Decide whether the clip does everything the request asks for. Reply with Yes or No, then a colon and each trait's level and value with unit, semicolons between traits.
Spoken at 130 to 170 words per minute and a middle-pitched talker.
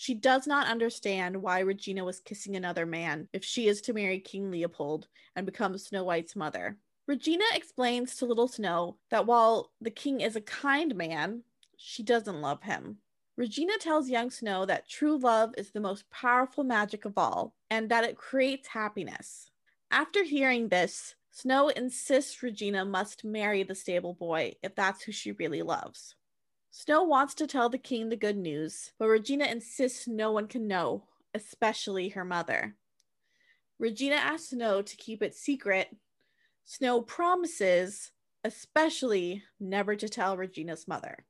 No: average, 160 wpm; high, 220 Hz